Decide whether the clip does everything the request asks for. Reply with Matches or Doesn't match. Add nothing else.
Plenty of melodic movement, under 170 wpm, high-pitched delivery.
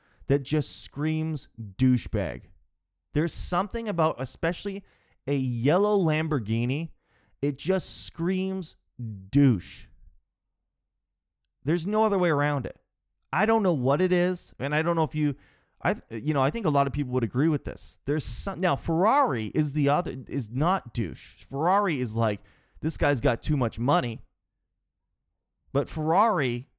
Doesn't match